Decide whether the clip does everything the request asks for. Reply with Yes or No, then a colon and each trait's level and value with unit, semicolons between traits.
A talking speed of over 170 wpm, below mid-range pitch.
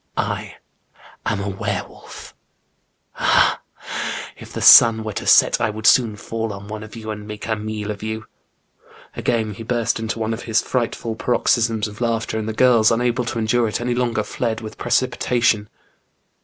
Yes: average, 185 wpm; low, 110 Hz